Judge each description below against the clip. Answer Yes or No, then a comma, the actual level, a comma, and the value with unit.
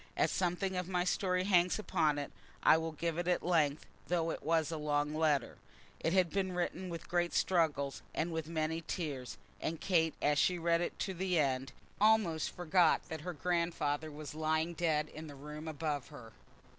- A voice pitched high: No, medium, 165 Hz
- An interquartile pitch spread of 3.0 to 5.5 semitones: No, narrow, 2.6 semitones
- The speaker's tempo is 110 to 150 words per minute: No, average, 190 wpm